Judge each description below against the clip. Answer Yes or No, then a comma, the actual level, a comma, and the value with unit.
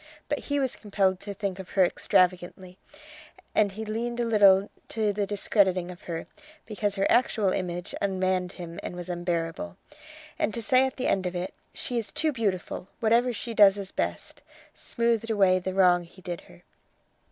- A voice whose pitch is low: No, high, 195 Hz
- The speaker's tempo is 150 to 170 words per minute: No, average, 180 wpm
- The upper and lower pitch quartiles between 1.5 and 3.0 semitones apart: No, average, 3.4 semitones